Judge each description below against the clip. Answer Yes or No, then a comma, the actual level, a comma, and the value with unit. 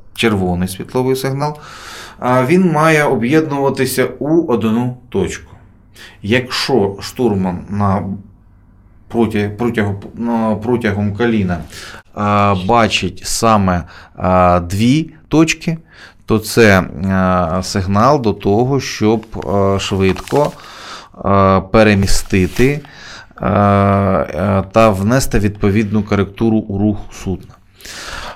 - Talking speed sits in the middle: No, slow, 70 wpm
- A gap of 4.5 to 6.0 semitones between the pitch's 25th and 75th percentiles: No, average, 3.8 semitones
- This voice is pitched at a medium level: No, low, 105 Hz